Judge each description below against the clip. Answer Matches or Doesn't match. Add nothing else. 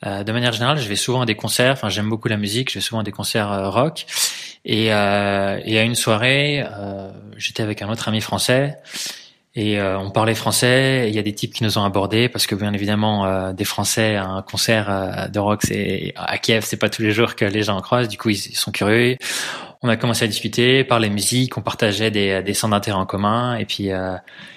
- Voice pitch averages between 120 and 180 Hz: Doesn't match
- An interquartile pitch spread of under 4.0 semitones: Matches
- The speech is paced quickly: Matches